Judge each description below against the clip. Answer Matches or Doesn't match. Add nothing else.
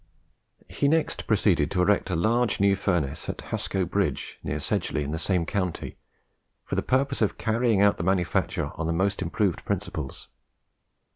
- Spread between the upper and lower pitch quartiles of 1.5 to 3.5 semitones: Doesn't match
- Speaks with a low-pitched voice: Matches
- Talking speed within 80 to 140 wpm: Doesn't match